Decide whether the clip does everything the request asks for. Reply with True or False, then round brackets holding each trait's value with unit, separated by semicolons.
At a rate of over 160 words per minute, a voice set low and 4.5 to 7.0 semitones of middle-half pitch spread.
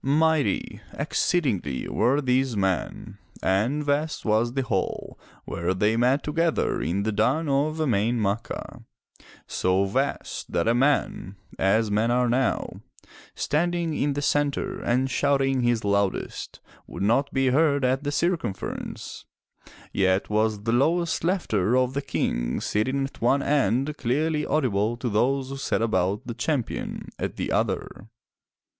False (140 wpm; 125 Hz; 5.1 semitones)